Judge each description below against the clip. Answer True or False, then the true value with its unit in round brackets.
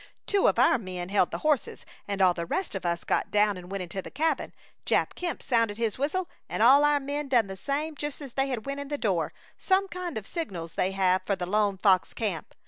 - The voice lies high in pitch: True (225 Hz)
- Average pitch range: False (7.3 semitones)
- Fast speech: True (235 wpm)